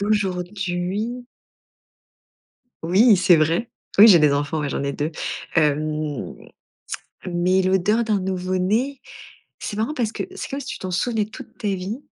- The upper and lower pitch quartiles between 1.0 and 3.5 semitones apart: No, average, 4.0 semitones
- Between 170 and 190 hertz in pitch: Yes, medium, 185 Hz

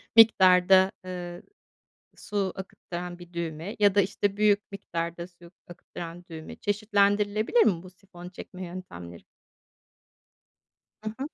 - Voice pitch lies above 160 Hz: Yes, medium, 185 Hz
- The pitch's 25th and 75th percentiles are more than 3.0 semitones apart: No, average, 2.7 semitones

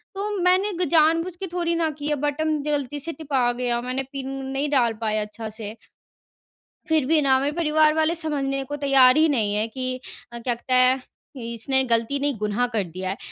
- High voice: Yes, very high, 275 Hz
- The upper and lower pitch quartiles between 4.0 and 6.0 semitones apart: Yes, average, 4.4 semitones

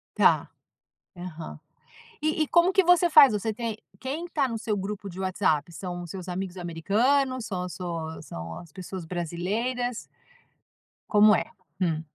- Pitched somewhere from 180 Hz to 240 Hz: Yes, high, 195 Hz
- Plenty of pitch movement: Yes, wide, 6.1 semitones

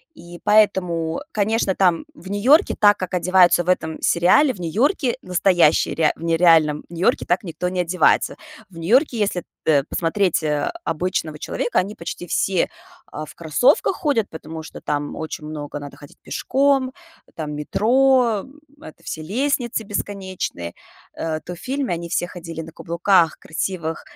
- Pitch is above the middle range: No, medium, 180 Hz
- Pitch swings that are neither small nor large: Yes, average, 4.4 semitones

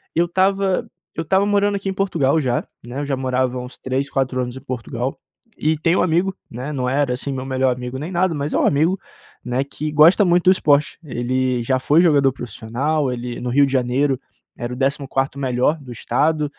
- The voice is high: No, medium, 140 Hz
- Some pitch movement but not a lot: Yes, average, 4.0 semitones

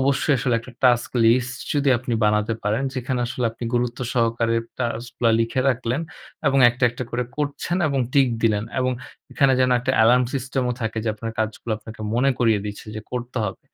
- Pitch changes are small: Yes, narrow, 2.2 semitones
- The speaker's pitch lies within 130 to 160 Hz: No, low, 120 Hz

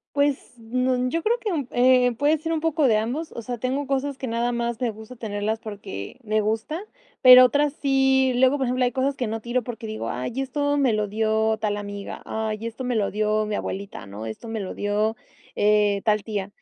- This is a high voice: Yes, high, 235 Hz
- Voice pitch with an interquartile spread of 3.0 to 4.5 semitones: Yes, average, 3.7 semitones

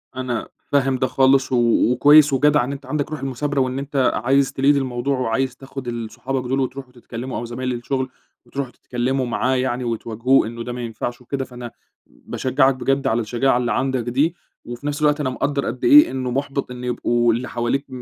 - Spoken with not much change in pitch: Yes, narrow, 2.0 semitones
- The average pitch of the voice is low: Yes, low, 130 Hz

